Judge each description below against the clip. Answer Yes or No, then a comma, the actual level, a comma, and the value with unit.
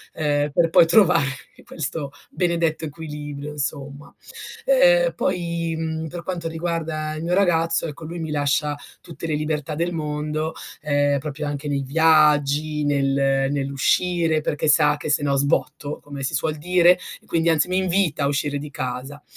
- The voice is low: No, medium, 155 Hz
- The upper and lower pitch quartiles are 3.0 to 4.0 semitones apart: No, narrow, 2.4 semitones